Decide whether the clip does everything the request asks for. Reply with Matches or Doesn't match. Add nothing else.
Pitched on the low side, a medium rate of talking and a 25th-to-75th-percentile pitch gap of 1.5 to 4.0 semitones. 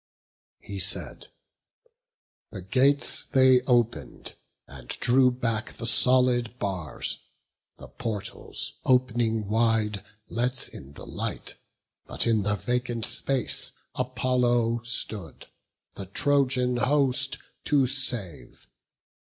Doesn't match